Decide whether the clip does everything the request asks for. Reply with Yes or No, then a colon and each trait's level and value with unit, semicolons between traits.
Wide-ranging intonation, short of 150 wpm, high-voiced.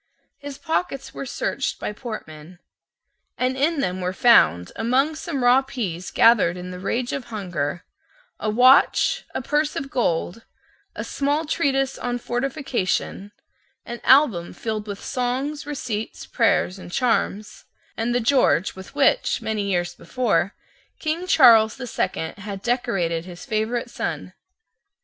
Yes: wide, 5.8 semitones; average, 140 wpm; high, 235 Hz